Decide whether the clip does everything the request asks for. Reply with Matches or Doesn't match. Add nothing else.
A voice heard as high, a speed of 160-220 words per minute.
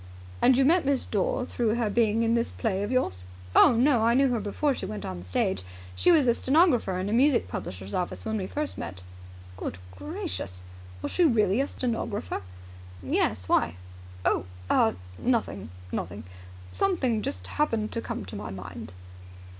Matches